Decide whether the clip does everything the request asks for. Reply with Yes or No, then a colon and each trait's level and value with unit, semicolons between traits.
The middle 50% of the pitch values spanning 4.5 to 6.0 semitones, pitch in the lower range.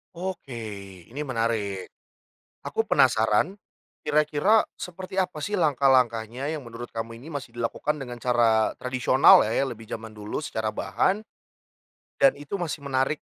Yes: average, 5.1 semitones; low, 130 Hz